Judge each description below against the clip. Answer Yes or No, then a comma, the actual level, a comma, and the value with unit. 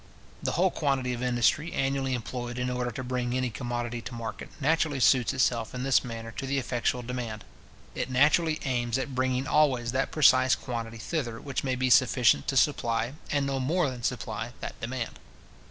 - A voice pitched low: Yes, low, 125 Hz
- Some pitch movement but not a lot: No, narrow, 2.1 semitones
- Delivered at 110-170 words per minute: No, average, 185 wpm